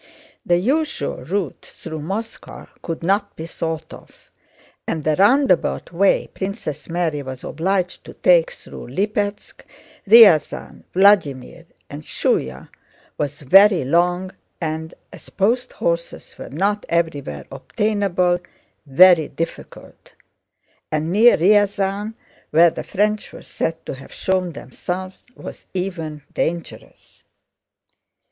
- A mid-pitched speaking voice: Yes, medium, 175 Hz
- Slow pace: Yes, slow, 115 wpm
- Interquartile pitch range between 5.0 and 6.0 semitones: No, average, 4.2 semitones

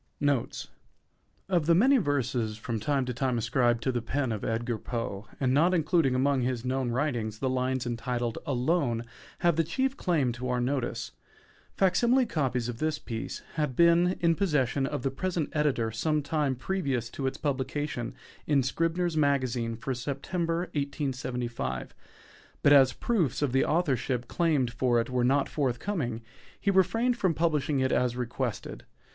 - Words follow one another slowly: No, average, 165 wpm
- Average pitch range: Yes, average, 4.5 semitones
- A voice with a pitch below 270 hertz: Yes, low, 135 Hz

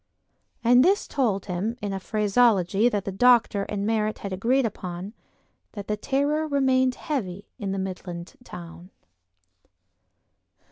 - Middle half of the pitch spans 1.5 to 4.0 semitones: No, average, 4.5 semitones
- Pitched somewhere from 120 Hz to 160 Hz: No, high, 210 Hz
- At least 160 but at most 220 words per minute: No, slow, 135 wpm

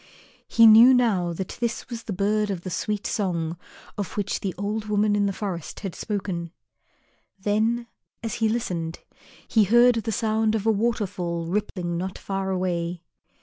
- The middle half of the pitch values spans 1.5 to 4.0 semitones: Yes, average, 3.4 semitones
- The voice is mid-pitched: No, high, 205 Hz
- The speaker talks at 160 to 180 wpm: Yes, average, 165 wpm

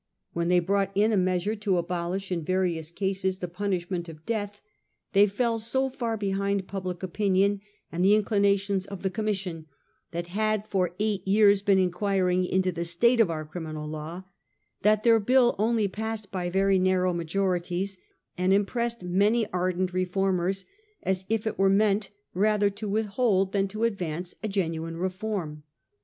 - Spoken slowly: No, average, 170 wpm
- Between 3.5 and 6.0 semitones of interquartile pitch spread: No, narrow, 2.5 semitones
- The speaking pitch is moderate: No, high, 195 Hz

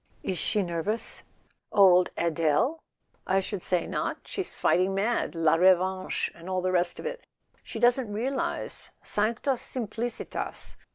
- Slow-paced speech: Yes, slow, 130 wpm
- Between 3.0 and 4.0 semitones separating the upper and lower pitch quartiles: No, average, 4.6 semitones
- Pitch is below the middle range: No, high, 195 Hz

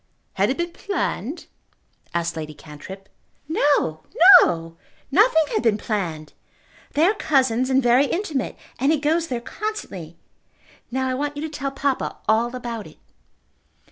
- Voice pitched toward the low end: No, very high, 255 Hz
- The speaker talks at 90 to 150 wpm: Yes, average, 145 wpm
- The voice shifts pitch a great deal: Yes, wide, 7.4 semitones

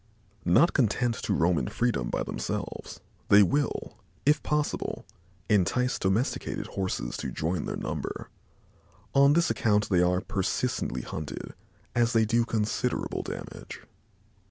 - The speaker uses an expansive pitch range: Yes, wide, 5.7 semitones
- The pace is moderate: No, slow, 130 wpm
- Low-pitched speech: Yes, low, 105 Hz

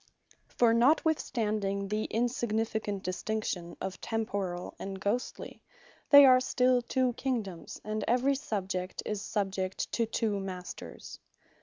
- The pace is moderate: No, slow, 115 wpm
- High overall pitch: Yes, high, 215 Hz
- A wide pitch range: No, average, 4.0 semitones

